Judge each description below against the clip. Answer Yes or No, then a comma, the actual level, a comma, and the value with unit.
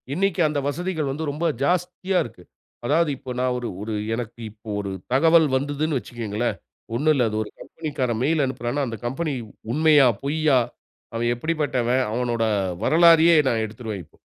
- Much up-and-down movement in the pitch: No, average, 4.9 semitones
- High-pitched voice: No, medium, 140 Hz